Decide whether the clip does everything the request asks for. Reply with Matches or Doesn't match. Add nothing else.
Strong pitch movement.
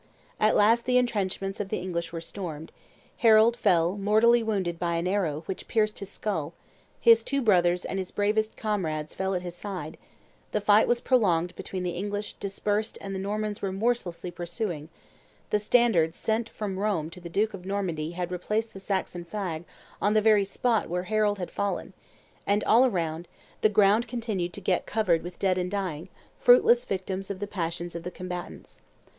Doesn't match